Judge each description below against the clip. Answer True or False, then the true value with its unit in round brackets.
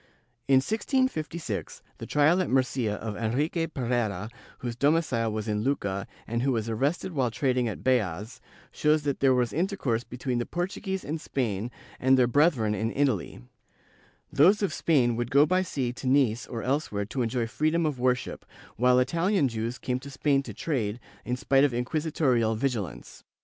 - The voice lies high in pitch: False (130 Hz)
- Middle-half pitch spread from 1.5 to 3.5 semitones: False (4.5 semitones)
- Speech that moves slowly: False (170 wpm)